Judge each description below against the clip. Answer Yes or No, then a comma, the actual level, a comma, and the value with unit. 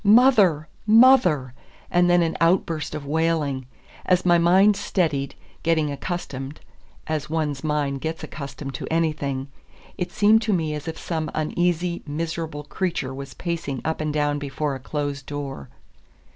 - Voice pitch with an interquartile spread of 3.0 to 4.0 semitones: Yes, average, 3.3 semitones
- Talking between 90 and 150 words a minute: Yes, average, 145 wpm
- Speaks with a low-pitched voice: No, medium, 155 Hz